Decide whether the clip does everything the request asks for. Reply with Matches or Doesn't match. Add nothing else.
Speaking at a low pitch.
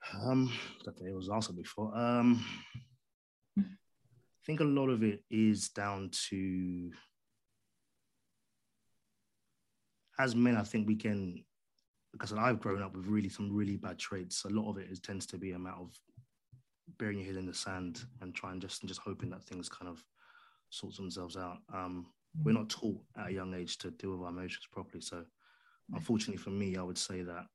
Matches